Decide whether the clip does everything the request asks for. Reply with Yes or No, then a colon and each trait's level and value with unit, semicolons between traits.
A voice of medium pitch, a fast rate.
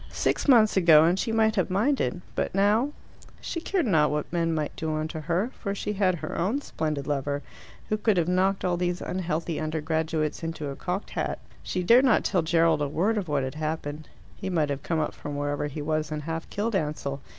Yes: medium, 165 Hz; fast, 215 wpm